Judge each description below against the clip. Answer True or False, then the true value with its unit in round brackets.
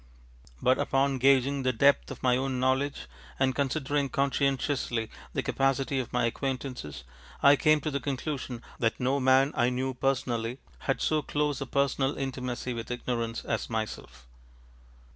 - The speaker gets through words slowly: False (150 wpm)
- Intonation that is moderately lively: False (1.9 semitones)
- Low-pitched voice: True (130 Hz)